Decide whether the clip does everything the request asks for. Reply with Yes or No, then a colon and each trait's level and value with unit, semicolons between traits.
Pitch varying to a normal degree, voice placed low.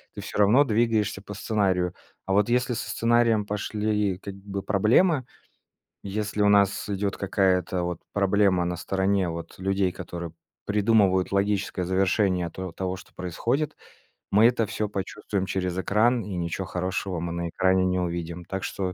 No: narrow, 2.3 semitones; low, 100 Hz